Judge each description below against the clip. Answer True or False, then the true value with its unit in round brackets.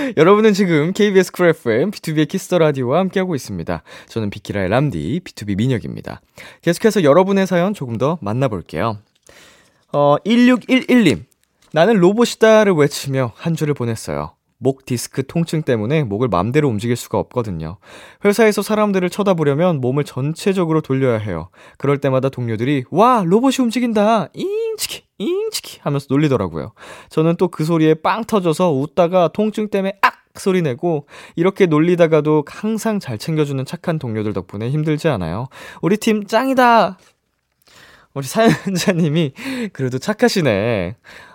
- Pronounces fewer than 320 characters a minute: False (350 characters per minute)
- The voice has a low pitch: False (160 Hz)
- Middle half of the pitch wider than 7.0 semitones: True (7.6 semitones)